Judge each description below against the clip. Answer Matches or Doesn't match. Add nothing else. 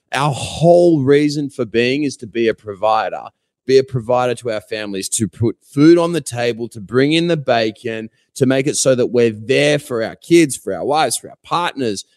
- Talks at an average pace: Doesn't match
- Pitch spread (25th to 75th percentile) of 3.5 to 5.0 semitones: Matches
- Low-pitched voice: Matches